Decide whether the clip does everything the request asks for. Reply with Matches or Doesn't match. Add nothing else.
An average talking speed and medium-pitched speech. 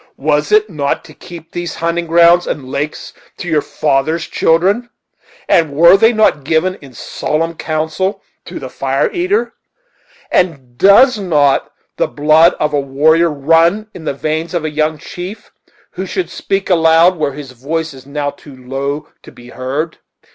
Matches